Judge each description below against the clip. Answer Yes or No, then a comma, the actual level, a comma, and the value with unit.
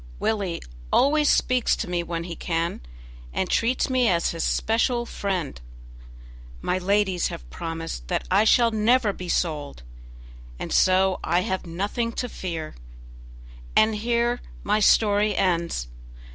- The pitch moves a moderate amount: Yes, average, 5.0 semitones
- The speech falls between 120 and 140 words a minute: Yes, slow, 135 wpm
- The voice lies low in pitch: No, high, 190 Hz